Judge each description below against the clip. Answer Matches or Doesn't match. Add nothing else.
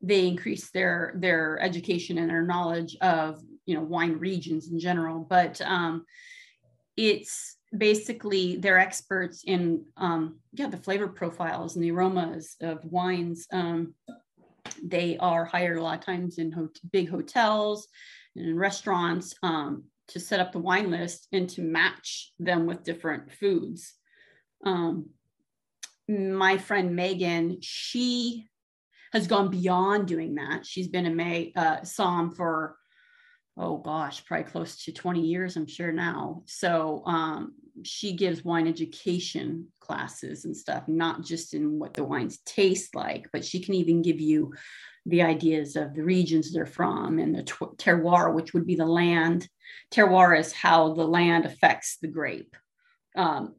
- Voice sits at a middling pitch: Matches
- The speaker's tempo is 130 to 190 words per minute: Matches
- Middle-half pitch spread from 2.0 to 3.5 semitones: Matches